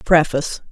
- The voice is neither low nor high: Yes, medium, 155 Hz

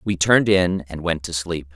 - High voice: No, very low, 85 Hz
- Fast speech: Yes, fast, 240 wpm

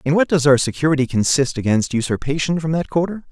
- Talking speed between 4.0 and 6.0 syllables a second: No, 6.3 syllables/s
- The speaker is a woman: No, male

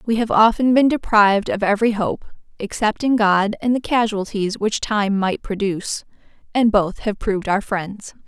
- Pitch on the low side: No, high, 210 Hz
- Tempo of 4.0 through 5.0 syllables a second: Yes, 4.8 syllables/s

